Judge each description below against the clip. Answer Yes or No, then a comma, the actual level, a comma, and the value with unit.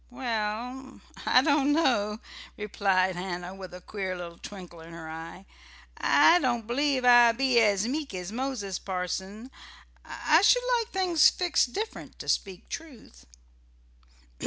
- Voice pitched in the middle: No, high, 220 Hz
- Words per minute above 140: No, slow, 135 wpm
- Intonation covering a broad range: Yes, wide, 6.3 semitones